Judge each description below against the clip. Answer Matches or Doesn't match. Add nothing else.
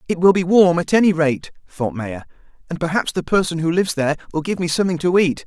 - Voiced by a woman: Doesn't match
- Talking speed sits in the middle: Doesn't match